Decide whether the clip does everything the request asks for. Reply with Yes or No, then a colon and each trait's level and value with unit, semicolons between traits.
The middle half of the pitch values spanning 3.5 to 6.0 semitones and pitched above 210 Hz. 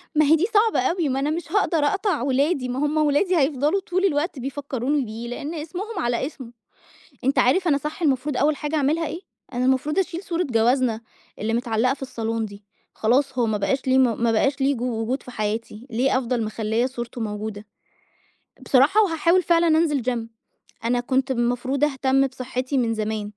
Yes: average, 4.1 semitones; very high, 265 Hz